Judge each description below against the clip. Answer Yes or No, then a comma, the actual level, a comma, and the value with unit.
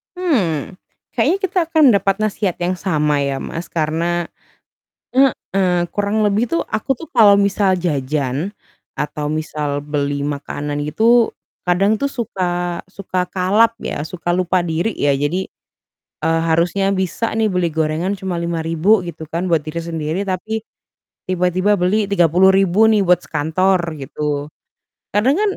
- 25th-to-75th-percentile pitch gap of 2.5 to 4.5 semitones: Yes, average, 4.0 semitones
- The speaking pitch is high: No, medium, 180 Hz